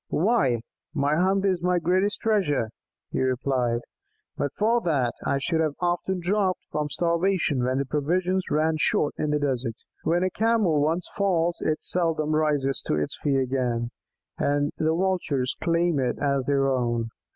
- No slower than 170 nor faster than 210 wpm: No, average, 160 wpm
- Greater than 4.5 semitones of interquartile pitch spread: Yes, average, 4.9 semitones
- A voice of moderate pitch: Yes, medium, 155 Hz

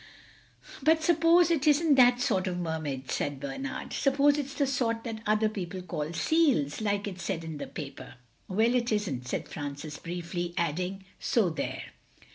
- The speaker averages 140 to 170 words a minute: Yes, average, 165 wpm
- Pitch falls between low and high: No, high, 195 Hz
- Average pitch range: No, wide, 8.5 semitones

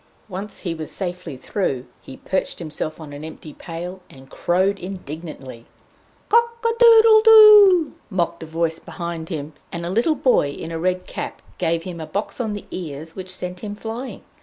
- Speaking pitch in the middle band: Yes, medium, 180 Hz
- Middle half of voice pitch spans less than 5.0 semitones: Yes, average, 4.6 semitones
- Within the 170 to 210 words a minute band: Yes, average, 180 wpm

